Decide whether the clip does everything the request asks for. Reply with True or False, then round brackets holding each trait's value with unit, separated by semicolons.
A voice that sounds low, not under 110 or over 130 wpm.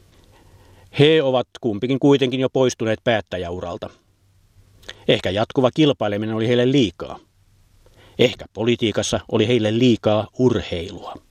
False (110 Hz; 100 wpm)